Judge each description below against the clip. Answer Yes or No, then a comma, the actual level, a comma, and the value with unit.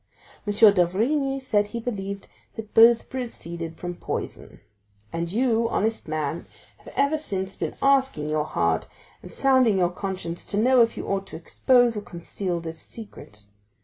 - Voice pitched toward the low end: No, high, 205 Hz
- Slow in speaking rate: No, average, 155 wpm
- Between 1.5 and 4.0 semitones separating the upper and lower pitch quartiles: No, wide, 5.6 semitones